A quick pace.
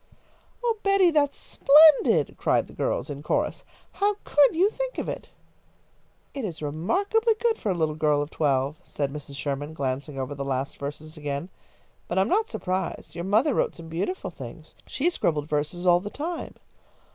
No: average, 180 wpm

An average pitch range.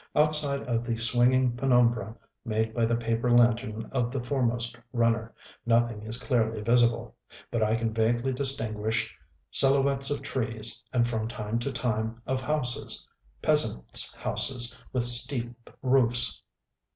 No: narrow, 1.9 semitones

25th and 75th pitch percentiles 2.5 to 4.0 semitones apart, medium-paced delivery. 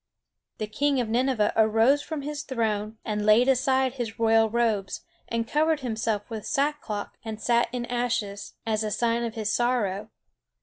Yes: average, 2.9 semitones; average, 170 wpm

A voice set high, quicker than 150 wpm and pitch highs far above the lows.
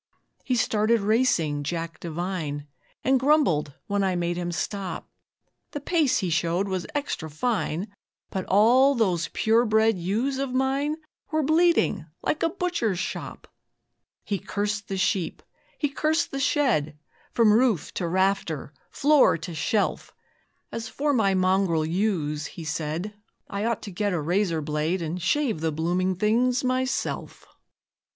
No: high, 200 Hz; average, 145 wpm; wide, 6.8 semitones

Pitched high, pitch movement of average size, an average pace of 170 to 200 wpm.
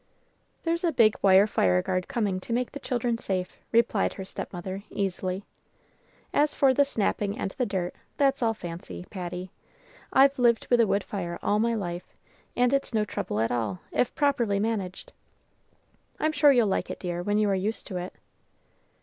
Yes: high, 205 Hz; average, 5.0 semitones; average, 175 wpm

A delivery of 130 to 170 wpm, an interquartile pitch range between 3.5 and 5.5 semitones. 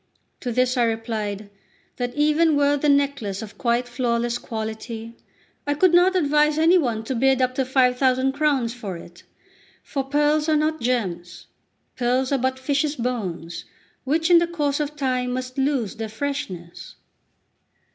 Yes: average, 160 wpm; average, 4.0 semitones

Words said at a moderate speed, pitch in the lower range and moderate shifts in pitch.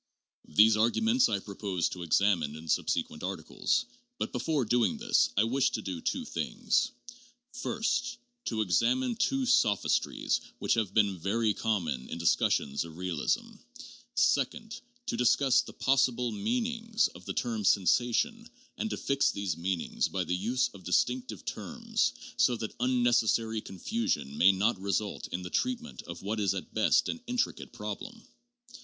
No: average, 150 wpm; low, 110 Hz; wide, 6.8 semitones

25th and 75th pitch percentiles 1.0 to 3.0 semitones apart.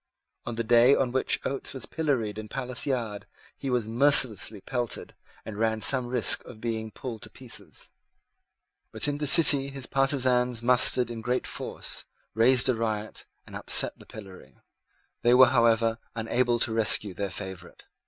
Yes: average, 2.7 semitones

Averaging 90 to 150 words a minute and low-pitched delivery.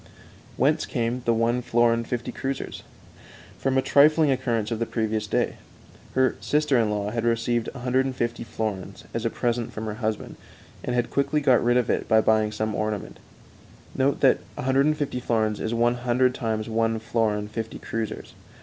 No: average, 165 wpm; low, 115 Hz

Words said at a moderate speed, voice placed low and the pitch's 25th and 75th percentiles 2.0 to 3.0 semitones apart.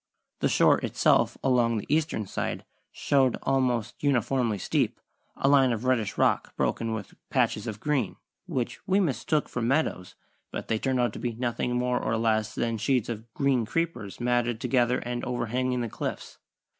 Yes: average, 170 wpm; low, 125 Hz; average, 2.7 semitones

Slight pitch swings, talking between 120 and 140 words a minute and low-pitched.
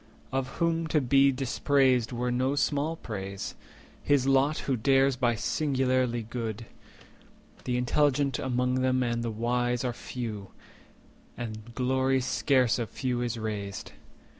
Yes: narrow, 2.3 semitones; slow, 135 wpm; low, 125 Hz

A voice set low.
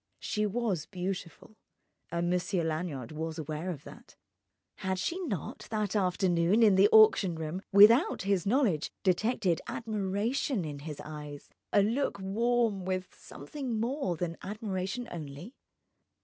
No: high, 190 Hz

